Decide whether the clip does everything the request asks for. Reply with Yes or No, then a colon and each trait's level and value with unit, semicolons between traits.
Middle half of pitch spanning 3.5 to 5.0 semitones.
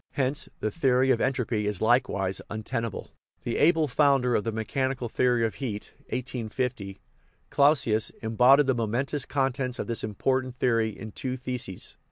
No: average, 3.1 semitones